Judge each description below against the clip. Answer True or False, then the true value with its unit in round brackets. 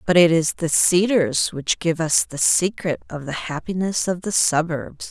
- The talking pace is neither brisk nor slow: True (190 wpm)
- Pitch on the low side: False (170 Hz)